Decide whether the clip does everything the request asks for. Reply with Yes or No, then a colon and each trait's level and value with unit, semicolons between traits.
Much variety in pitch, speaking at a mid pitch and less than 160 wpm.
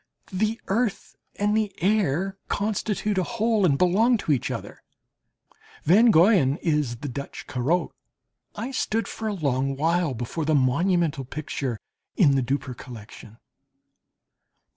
Yes: wide, 7.2 semitones; medium, 170 Hz; slow, 135 wpm